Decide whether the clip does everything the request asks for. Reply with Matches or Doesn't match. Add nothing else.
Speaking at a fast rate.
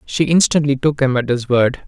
Matches